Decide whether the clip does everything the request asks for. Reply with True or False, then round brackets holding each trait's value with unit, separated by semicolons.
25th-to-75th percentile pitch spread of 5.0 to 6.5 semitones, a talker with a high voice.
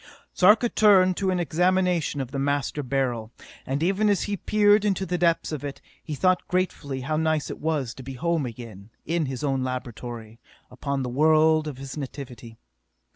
False (5.5 semitones; 150 Hz)